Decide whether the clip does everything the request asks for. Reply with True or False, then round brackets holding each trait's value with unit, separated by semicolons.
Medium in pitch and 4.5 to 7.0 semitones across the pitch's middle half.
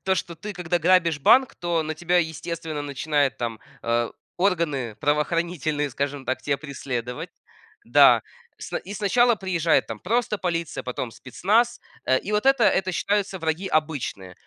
True (165 Hz; 4.8 semitones)